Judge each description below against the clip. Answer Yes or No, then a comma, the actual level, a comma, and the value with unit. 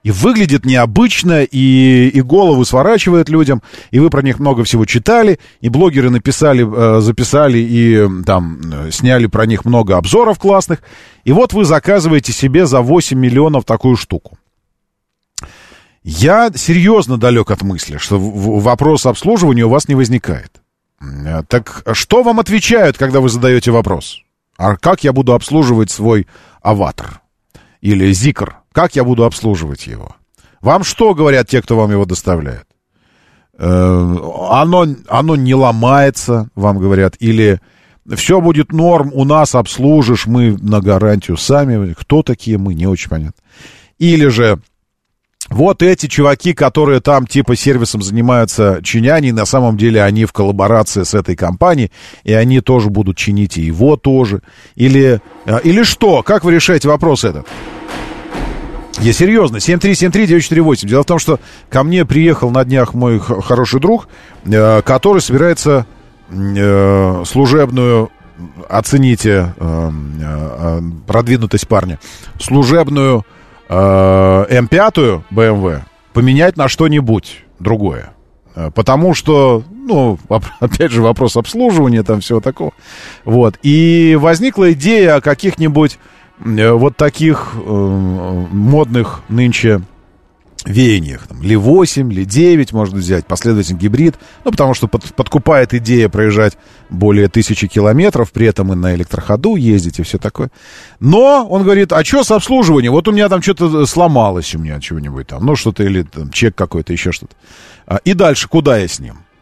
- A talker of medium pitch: No, low, 120 Hz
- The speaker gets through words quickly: No, average, 135 wpm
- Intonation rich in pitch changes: Yes, wide, 6.7 semitones